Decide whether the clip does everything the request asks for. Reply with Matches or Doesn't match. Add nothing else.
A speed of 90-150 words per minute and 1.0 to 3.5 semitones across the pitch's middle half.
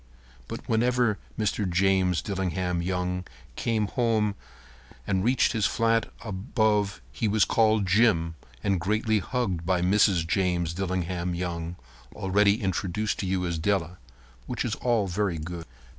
Matches